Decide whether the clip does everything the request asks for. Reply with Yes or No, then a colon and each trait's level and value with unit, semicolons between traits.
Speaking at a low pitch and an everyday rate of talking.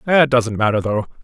Yes: low, 120 Hz; average, 195 wpm